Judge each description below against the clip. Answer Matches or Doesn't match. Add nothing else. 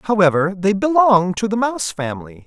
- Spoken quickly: Doesn't match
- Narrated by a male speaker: Matches